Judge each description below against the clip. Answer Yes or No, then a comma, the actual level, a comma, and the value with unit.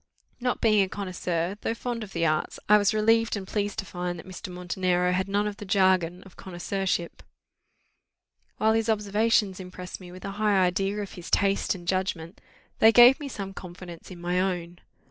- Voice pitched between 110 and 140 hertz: No, high, 190 Hz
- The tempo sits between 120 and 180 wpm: No, average, 190 wpm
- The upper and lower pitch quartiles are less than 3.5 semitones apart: Yes, average, 2.7 semitones